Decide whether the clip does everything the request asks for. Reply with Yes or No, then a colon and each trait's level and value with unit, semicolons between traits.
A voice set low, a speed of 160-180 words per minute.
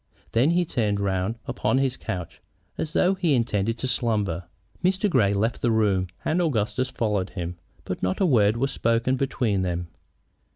Yes: low, 115 Hz; average, 170 wpm